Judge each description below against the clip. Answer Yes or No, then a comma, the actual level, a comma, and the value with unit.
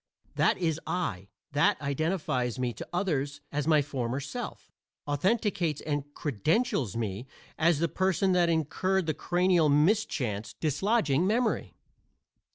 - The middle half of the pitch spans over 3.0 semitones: Yes, average, 4.7 semitones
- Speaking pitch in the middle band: Yes, medium, 155 Hz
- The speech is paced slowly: Yes, slow, 125 wpm